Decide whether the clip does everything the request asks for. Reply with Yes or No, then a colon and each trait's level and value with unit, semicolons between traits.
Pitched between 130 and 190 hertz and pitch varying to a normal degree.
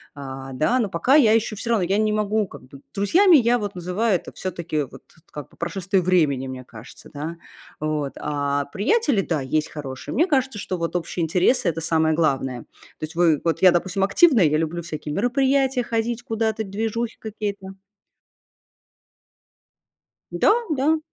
No: medium, 185 Hz; wide, 6.5 semitones